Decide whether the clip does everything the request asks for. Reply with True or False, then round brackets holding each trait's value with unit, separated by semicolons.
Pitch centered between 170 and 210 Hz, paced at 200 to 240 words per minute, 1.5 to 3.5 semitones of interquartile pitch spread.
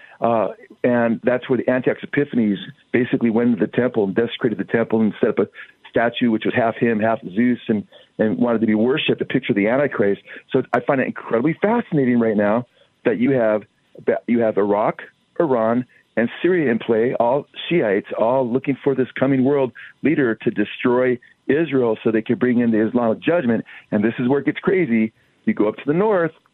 False (120 Hz; 205 wpm; 2.9 semitones)